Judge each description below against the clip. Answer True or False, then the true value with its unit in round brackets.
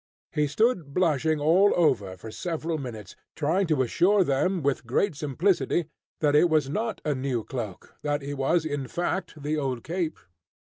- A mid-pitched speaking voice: True (150 Hz)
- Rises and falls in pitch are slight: False (4.2 semitones)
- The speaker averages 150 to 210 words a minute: True (170 wpm)